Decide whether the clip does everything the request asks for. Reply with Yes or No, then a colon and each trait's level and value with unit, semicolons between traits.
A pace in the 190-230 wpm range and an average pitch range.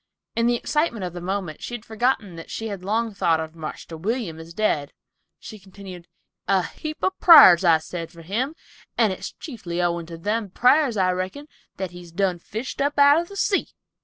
No: average, 200 wpm; wide, 5.7 semitones